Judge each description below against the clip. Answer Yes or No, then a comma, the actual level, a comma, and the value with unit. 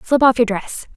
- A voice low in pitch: No, high, 235 Hz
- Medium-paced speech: No, fast, 250 wpm